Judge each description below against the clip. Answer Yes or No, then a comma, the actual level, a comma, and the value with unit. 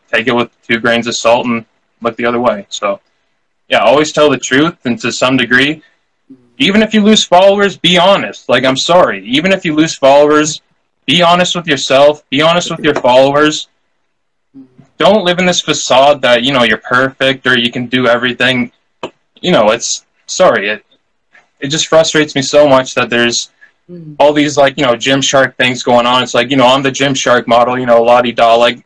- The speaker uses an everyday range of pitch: Yes, average, 4.1 semitones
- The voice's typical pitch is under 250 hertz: Yes, low, 135 Hz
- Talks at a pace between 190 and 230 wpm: Yes, fast, 205 wpm